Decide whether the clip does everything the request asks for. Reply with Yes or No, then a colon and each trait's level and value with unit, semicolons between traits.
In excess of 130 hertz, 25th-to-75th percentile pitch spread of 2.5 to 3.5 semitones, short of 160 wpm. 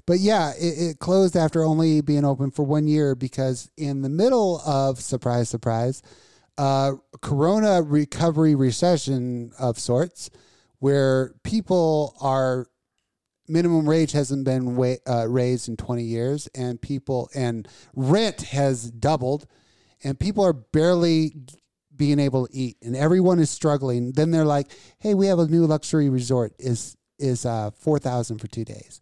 No: medium, 140 Hz; average, 4.0 semitones; average, 150 wpm